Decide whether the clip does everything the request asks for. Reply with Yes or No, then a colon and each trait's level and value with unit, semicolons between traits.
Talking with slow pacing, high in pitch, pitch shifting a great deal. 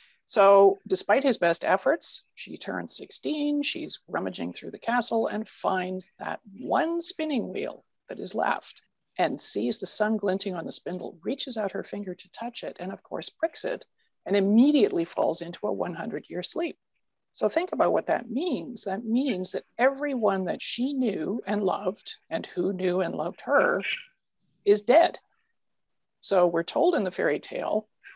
No: average, 170 wpm; high, 220 Hz; wide, 7.1 semitones